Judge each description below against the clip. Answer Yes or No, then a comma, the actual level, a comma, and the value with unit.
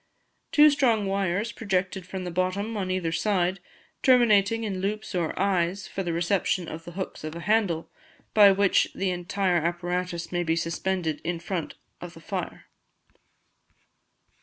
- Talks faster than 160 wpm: No, average, 155 wpm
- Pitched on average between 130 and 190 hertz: Yes, medium, 185 Hz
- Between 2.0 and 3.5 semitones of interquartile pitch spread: Yes, narrow, 2.6 semitones